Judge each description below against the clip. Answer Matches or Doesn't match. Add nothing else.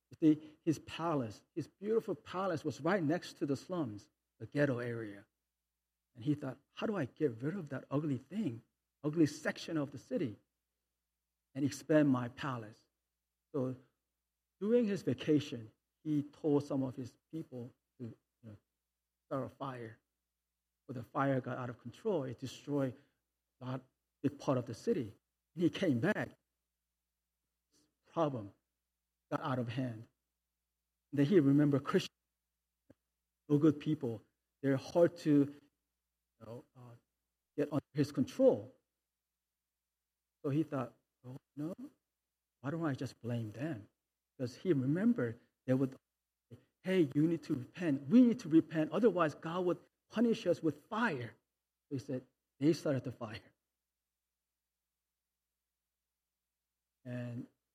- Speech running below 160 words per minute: Matches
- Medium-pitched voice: Doesn't match